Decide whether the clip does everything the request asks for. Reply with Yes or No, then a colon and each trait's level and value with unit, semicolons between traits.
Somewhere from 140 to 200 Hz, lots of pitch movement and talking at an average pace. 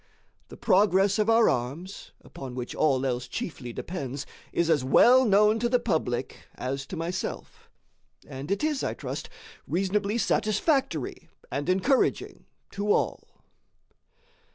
No: medium, 185 Hz; wide, 7.8 semitones; slow, 130 wpm